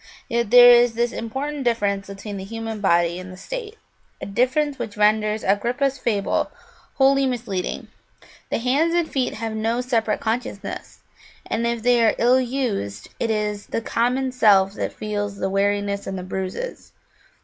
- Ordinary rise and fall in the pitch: Yes, average, 3.7 semitones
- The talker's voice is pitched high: Yes, high, 225 Hz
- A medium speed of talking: Yes, average, 160 wpm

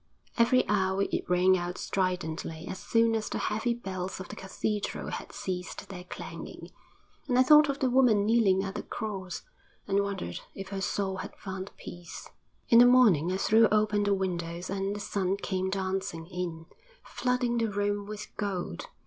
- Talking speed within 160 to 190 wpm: Yes, average, 175 wpm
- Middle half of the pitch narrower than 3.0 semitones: Yes, narrow, 2.6 semitones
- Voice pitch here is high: Yes, high, 195 Hz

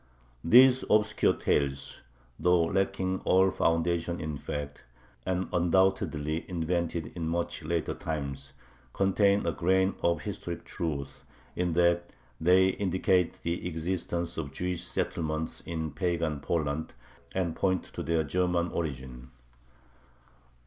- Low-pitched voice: Yes, very low, 85 Hz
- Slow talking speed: Yes, slow, 115 wpm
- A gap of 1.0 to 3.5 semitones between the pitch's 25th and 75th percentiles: Yes, narrow, 2.6 semitones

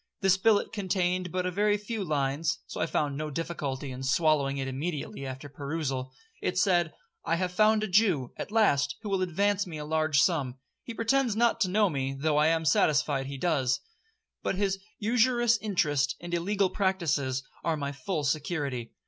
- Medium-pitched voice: Yes, medium, 165 Hz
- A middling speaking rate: Yes, average, 180 wpm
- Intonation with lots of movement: Yes, wide, 6.0 semitones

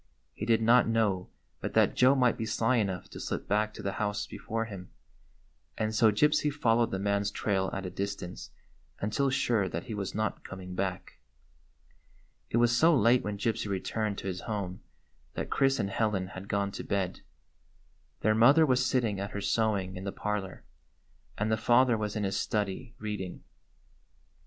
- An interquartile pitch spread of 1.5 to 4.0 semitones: Yes, average, 2.8 semitones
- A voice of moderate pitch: No, low, 105 Hz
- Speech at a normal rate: Yes, average, 180 wpm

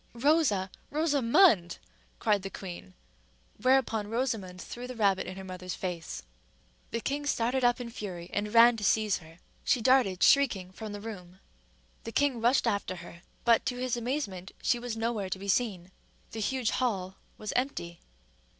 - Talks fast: No, average, 170 wpm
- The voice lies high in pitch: Yes, high, 220 Hz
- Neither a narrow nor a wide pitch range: Yes, average, 4.8 semitones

